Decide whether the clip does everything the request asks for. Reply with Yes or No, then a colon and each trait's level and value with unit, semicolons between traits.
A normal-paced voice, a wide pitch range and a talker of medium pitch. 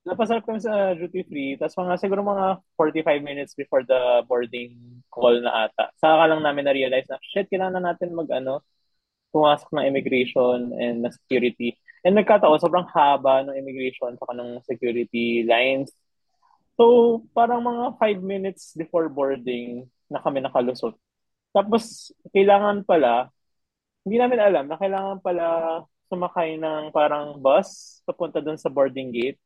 Yes: average, 145 wpm; wide, 6.9 semitones; medium, 155 Hz